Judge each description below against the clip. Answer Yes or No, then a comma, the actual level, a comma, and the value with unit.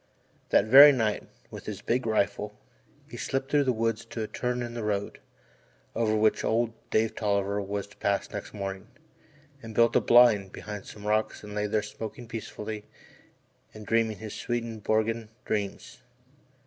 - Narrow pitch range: Yes, narrow, 1.9 semitones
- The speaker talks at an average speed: Yes, average, 160 wpm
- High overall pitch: No, low, 110 Hz